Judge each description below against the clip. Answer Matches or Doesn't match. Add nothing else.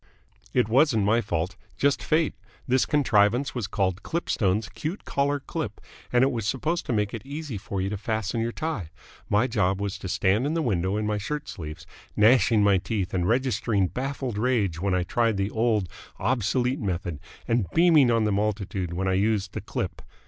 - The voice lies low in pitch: Matches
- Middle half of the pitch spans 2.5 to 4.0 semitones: Doesn't match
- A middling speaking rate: Matches